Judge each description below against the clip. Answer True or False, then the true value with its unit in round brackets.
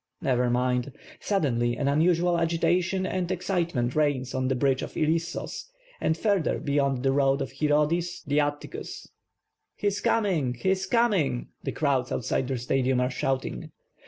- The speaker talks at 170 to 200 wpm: False (160 wpm)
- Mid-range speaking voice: True (145 Hz)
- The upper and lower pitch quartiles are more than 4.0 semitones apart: True (5.1 semitones)